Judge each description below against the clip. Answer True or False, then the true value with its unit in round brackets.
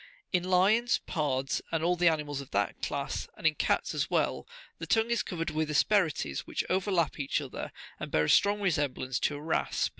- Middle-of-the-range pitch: True (160 Hz)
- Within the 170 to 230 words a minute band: True (200 wpm)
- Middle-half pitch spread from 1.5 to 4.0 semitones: False (4.6 semitones)